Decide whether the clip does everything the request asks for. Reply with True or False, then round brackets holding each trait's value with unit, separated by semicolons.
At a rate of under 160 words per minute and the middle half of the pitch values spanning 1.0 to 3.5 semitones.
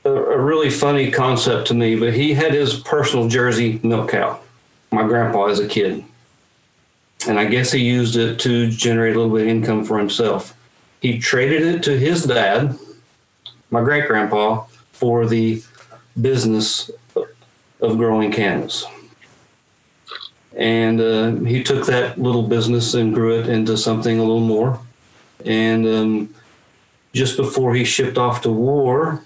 True (150 wpm; 2.6 semitones)